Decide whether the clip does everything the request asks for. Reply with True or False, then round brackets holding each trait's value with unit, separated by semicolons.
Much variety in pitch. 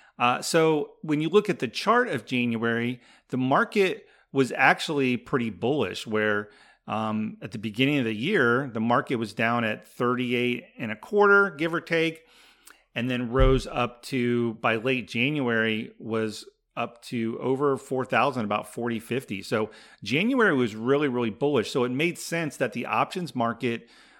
False (4.0 semitones)